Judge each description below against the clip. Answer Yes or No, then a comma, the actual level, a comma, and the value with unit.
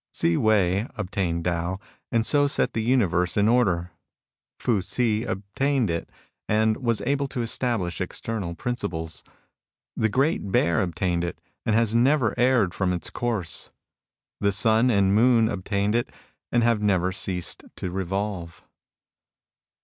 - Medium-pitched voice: No, low, 105 Hz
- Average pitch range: Yes, average, 4.5 semitones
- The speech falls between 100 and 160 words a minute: Yes, average, 150 wpm